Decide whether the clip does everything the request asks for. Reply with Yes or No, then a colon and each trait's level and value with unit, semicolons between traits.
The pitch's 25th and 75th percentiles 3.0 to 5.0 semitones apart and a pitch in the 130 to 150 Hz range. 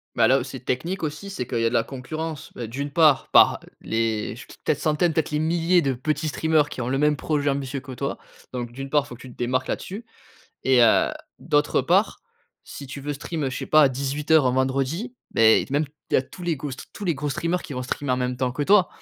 Yes: average, 3.5 semitones; medium, 140 Hz